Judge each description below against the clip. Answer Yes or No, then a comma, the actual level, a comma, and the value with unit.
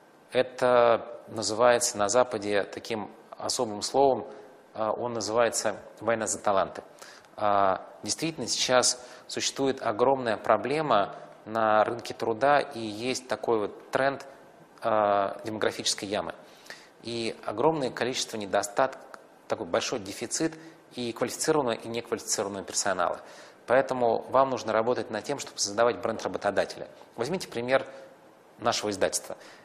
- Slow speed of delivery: Yes, slow, 105 wpm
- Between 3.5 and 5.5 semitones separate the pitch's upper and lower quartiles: No, average, 3.0 semitones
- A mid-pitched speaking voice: No, low, 120 Hz